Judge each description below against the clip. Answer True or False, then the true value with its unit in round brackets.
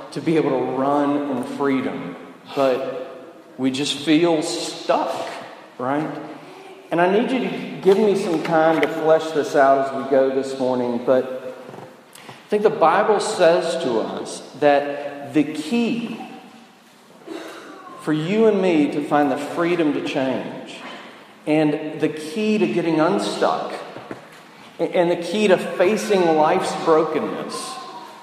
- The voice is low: False (160 Hz)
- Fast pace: False (140 wpm)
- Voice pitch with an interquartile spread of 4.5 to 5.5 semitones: True (5.2 semitones)